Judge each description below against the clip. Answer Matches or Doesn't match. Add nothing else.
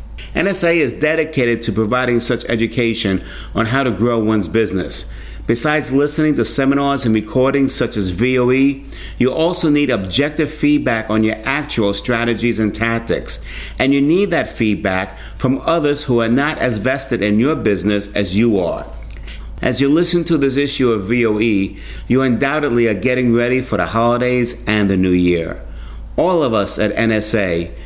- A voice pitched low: Matches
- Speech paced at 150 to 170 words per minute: Matches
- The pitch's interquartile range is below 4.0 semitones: Doesn't match